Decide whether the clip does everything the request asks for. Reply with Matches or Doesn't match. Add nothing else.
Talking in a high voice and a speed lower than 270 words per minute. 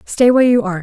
Doesn't match